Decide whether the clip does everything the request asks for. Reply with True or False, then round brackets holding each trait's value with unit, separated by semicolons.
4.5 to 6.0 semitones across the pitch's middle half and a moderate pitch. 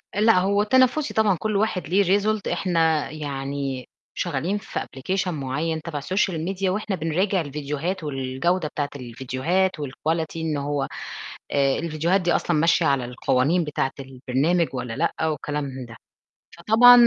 True (5.2 semitones; 160 Hz)